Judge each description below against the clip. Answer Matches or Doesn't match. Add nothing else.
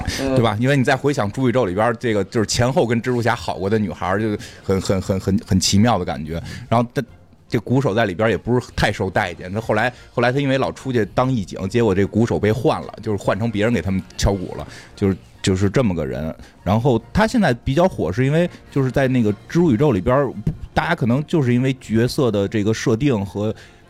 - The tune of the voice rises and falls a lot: Doesn't match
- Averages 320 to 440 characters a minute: Matches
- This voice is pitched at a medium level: Doesn't match